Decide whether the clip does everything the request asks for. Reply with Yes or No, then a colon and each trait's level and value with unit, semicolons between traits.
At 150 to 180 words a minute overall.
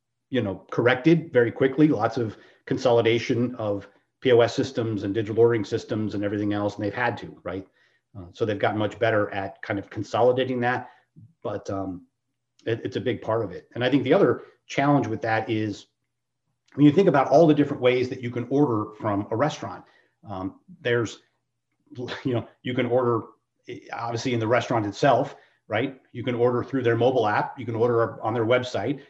No: average, 190 wpm